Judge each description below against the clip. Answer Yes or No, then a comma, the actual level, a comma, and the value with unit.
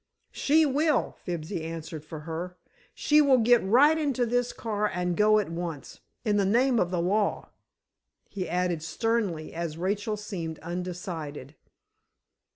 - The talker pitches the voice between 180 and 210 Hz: Yes, high, 190 Hz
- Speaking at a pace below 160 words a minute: Yes, average, 140 wpm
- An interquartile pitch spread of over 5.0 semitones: Yes, wide, 5.6 semitones